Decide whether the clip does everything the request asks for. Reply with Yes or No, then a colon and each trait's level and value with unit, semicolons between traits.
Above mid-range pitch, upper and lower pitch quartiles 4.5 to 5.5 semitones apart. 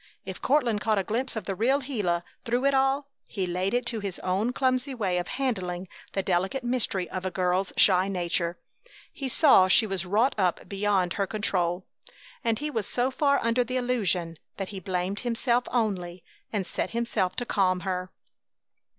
Yes: high, 205 Hz; average, 5.0 semitones